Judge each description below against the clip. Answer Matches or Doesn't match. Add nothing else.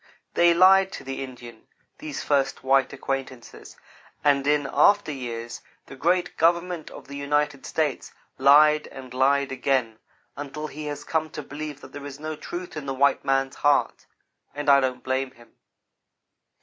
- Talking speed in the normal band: Matches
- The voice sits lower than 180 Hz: Matches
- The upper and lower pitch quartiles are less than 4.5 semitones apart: Matches